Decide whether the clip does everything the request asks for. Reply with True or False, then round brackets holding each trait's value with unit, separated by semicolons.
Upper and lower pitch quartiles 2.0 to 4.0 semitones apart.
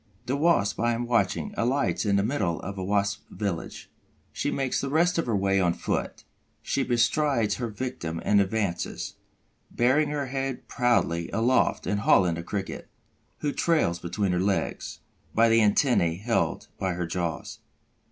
False (5.4 semitones)